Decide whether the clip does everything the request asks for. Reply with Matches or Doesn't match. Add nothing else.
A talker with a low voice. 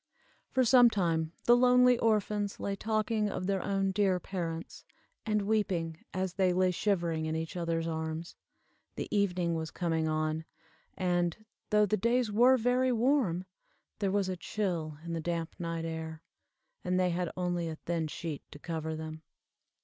Doesn't match